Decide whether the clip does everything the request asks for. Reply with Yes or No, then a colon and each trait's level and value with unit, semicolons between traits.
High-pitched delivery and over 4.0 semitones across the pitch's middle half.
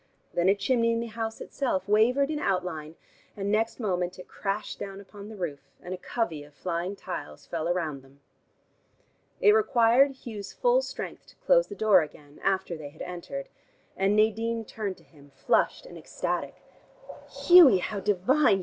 Yes: high, 200 Hz; average, 4.7 semitones